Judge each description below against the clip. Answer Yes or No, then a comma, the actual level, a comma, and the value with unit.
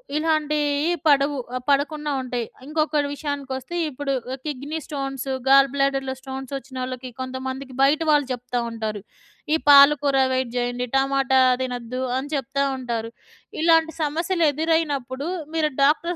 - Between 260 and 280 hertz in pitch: Yes, very high, 275 Hz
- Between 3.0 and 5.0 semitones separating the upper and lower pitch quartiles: No, narrow, 2.5 semitones